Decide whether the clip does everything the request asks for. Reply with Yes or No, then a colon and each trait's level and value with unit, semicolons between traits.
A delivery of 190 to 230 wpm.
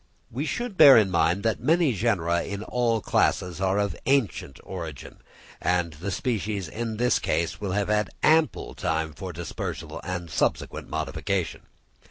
No: average, 155 wpm